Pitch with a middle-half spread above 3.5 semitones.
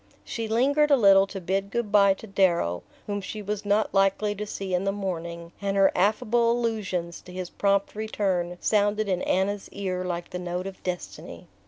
No: narrow, 2.5 semitones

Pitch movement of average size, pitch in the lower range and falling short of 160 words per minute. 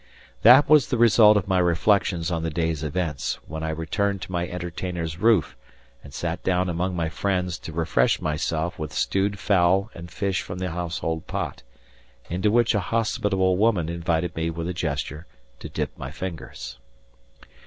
No: average, 3.1 semitones; very low, 90 Hz; average, 170 wpm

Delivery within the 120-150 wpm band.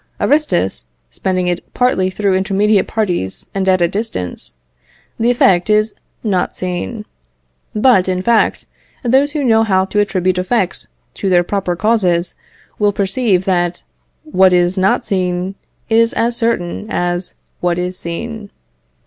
Yes: average, 140 wpm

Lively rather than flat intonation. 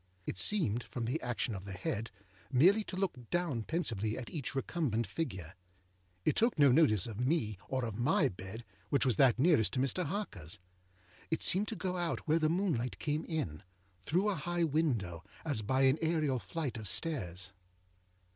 Yes: wide, 7.0 semitones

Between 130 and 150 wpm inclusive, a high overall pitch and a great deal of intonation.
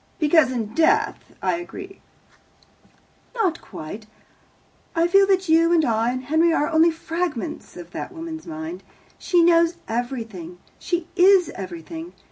Yes: slow, 135 wpm; very high, 325 Hz; wide, 6.1 semitones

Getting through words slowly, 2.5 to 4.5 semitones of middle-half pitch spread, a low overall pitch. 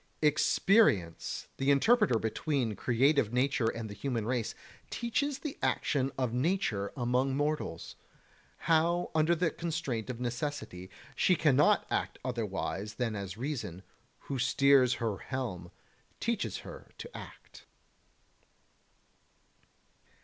No: slow, 115 wpm; wide, 5.5 semitones; low, 130 Hz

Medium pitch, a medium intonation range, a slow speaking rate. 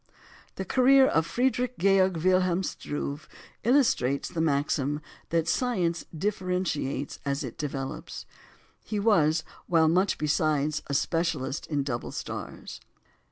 Yes: medium, 165 Hz; average, 4.5 semitones; slow, 115 wpm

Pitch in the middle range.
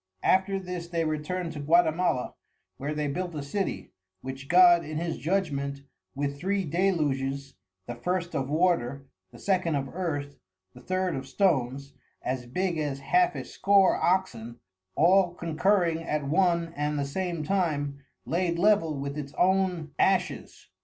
Yes: medium, 165 Hz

